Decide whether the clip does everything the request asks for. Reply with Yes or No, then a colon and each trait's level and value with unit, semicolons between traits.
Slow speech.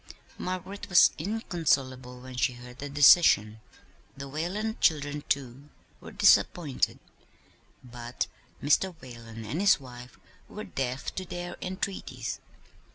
Yes: slow, 115 wpm